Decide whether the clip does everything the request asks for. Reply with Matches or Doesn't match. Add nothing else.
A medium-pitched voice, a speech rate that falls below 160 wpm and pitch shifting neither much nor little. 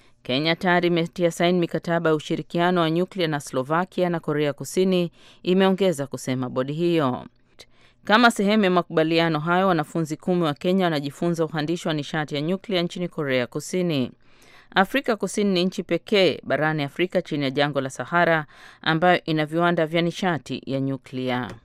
Matches